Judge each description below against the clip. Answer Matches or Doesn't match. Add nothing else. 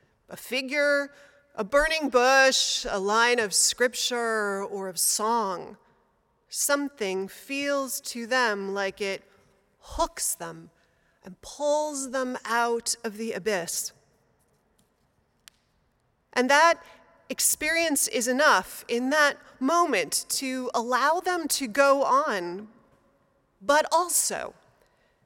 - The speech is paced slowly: Matches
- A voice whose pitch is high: Matches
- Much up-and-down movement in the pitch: Doesn't match